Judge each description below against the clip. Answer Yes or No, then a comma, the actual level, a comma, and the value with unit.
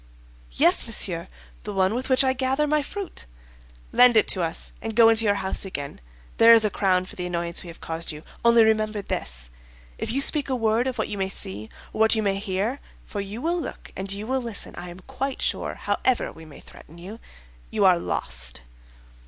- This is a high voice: Yes, high, 205 Hz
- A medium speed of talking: No, fast, 210 wpm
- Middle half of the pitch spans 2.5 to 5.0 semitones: No, wide, 5.4 semitones